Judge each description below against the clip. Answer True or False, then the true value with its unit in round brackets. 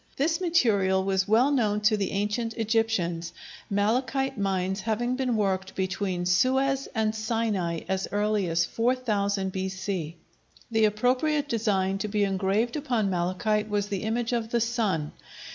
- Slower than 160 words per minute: True (145 wpm)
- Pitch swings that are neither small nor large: True (3.6 semitones)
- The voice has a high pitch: True (210 Hz)